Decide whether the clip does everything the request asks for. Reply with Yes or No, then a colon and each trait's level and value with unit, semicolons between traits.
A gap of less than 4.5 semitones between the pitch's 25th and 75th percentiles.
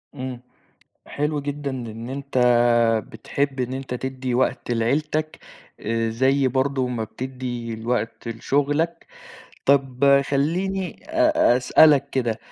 Yes: average, 2.7 semitones